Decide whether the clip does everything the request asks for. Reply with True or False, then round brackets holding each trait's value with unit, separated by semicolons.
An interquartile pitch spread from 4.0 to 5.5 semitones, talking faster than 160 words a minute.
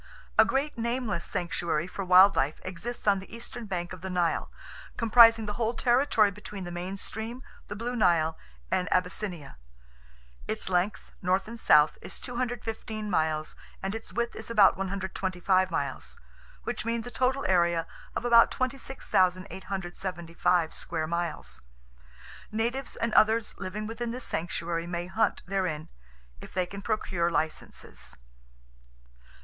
False (4.7 semitones; 135 wpm)